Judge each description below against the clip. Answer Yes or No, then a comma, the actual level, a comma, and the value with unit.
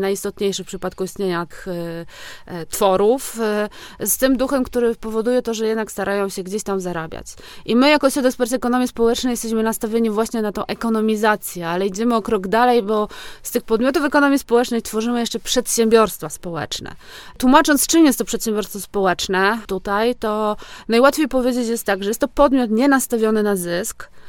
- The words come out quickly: Yes, fast, 170 wpm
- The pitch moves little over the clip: No, average, 3.6 semitones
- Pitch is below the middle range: No, high, 225 Hz